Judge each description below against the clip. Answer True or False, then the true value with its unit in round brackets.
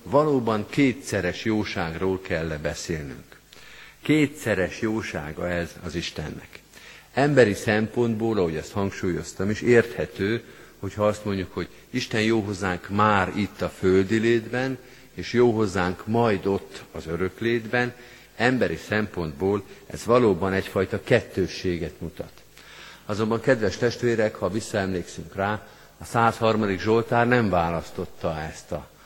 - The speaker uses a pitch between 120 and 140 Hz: False (105 Hz)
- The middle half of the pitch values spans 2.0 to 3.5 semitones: False (4.2 semitones)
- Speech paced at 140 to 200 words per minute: False (115 wpm)